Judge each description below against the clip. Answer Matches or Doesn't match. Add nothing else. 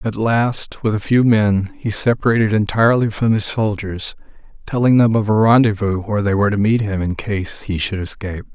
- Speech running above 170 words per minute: Matches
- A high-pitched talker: Doesn't match